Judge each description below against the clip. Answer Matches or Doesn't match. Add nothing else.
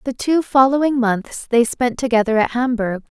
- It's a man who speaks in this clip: Doesn't match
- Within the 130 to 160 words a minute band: Doesn't match